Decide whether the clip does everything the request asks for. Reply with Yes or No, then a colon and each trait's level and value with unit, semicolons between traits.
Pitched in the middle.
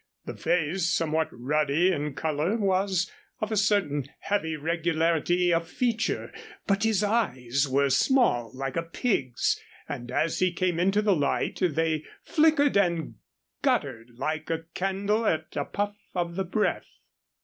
Yes: medium, 170 Hz